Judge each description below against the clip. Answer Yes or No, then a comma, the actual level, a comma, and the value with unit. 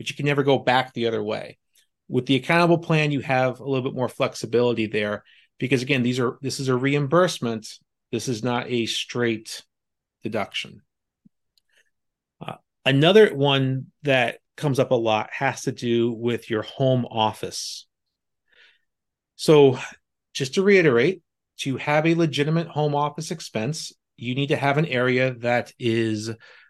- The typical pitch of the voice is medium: No, low, 130 Hz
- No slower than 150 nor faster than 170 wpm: Yes, average, 155 wpm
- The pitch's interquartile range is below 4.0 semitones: Yes, average, 3.5 semitones